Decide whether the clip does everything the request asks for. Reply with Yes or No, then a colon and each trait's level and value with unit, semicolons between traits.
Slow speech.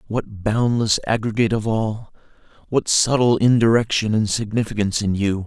Yes: slow, 130 wpm